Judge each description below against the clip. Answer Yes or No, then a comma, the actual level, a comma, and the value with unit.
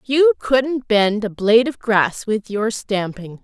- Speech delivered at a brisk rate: No, average, 175 wpm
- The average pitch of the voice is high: Yes, high, 215 Hz